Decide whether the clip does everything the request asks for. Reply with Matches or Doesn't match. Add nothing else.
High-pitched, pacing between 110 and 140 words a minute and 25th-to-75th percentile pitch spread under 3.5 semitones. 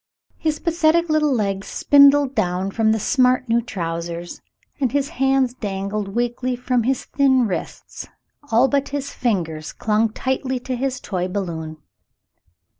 Doesn't match